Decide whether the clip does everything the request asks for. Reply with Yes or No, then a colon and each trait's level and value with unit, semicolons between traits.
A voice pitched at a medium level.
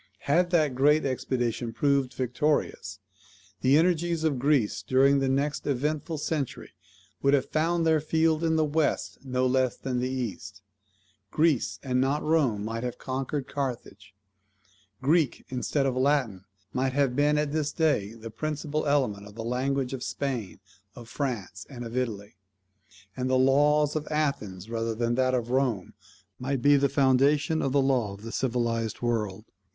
No: low, 130 Hz